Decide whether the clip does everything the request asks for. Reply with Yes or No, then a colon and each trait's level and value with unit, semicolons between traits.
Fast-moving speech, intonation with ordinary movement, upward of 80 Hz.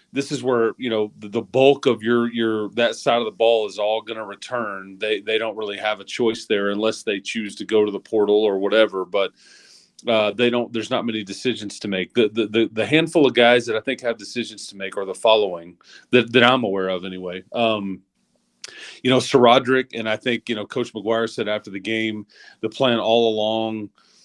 No: fast, 225 wpm; narrow, 2.2 semitones; low, 110 Hz